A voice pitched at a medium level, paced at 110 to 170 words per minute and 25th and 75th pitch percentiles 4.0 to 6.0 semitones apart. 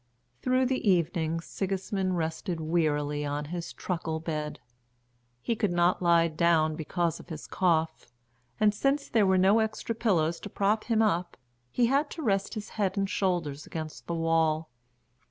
Yes: medium, 175 Hz; average, 160 wpm; average, 4.3 semitones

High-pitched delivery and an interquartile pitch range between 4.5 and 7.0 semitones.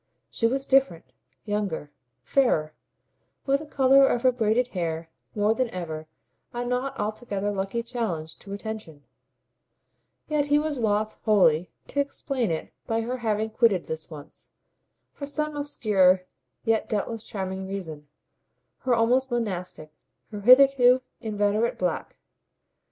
Yes: high, 220 Hz; average, 5.0 semitones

